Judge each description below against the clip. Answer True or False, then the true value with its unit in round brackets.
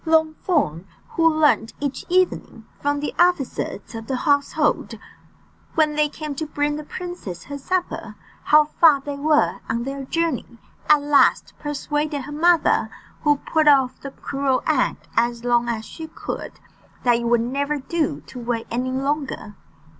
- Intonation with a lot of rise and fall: False (3.6 semitones)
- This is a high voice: True (285 Hz)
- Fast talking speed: False (155 wpm)